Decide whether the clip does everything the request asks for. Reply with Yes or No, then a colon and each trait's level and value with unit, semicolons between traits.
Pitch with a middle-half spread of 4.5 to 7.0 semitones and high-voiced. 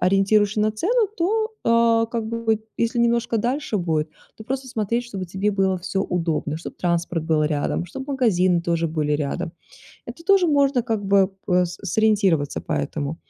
Yes: average, 5.3 semitones; high, 205 Hz